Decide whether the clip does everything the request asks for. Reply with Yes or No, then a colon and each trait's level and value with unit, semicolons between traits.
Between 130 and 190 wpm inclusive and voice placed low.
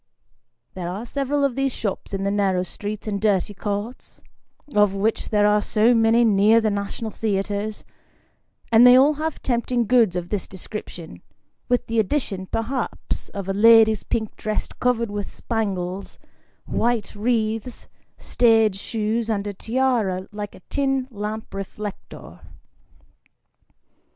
No: average, 140 wpm; high, 215 Hz